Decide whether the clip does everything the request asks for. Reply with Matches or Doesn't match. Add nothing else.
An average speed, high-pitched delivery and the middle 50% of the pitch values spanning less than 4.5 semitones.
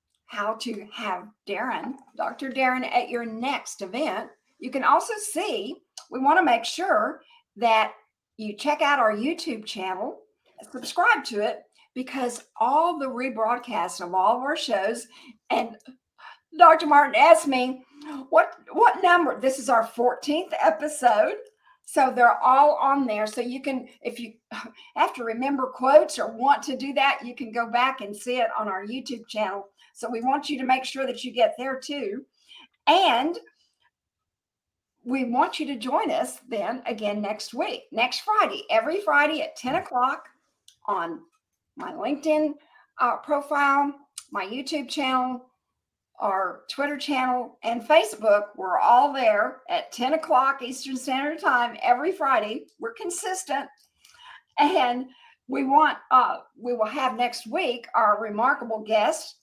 Doesn't match